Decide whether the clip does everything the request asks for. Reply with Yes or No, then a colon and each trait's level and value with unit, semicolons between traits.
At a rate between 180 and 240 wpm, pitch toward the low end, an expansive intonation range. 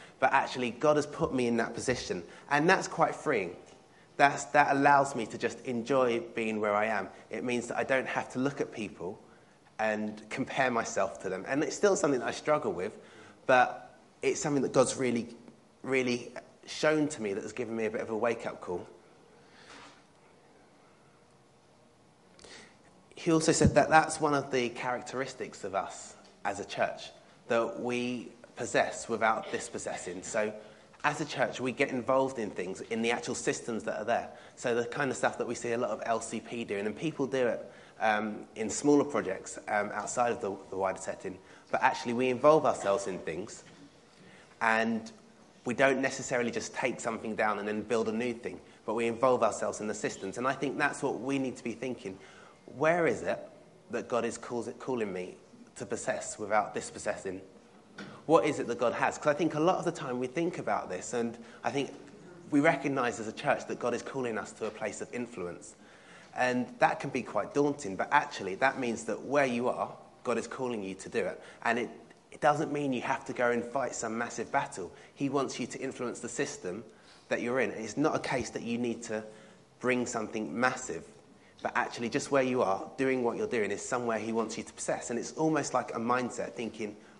No: fast, 205 wpm; low, 125 Hz; average, 3.7 semitones